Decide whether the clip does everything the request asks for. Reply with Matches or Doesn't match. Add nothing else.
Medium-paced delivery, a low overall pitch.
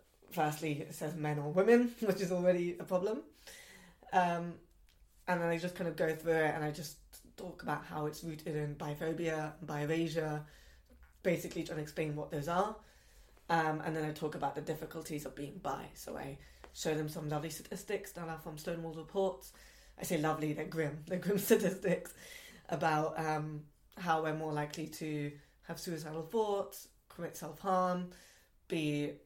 Doesn't match